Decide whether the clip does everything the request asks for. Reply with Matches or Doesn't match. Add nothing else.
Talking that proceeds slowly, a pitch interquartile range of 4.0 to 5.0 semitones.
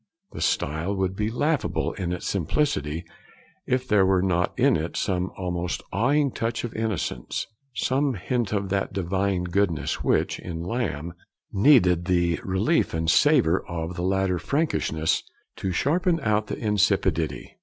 Doesn't match